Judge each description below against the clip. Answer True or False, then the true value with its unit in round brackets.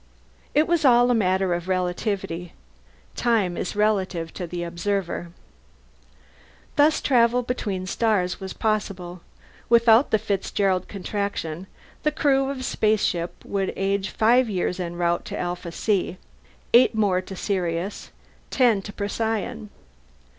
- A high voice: True (200 Hz)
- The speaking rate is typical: False (130 wpm)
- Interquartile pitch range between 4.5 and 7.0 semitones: False (4.0 semitones)